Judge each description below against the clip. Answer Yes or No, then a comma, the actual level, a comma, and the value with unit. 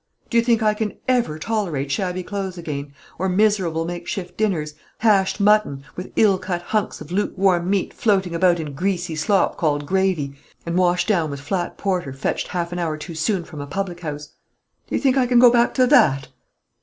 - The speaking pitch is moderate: Yes, medium, 180 Hz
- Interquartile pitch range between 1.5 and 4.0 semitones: No, average, 4.4 semitones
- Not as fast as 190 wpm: No, average, 200 wpm